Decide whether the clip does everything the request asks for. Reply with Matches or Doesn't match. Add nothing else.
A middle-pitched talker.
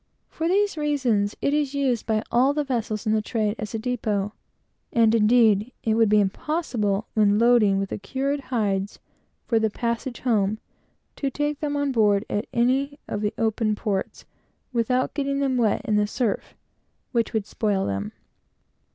Doesn't match